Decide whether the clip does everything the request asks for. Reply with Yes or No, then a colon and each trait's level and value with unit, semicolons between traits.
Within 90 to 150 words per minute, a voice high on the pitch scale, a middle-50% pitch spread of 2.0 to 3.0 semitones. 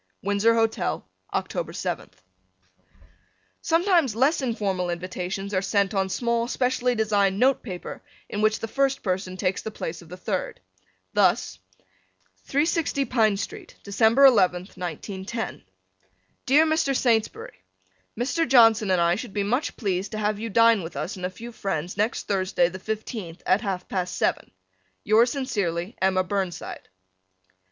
No: average, 145 wpm; high, 210 Hz; average, 4.5 semitones